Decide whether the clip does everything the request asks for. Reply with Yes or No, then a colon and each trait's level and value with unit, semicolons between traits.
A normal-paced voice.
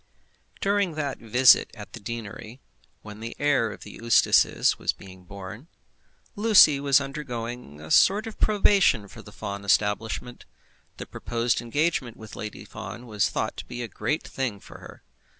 Yes: average, 160 wpm